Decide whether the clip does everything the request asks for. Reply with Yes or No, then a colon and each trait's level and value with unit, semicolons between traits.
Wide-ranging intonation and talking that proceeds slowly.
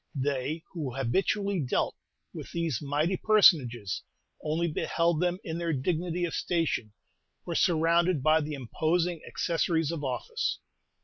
No: average, 3.2 semitones; slow, 130 wpm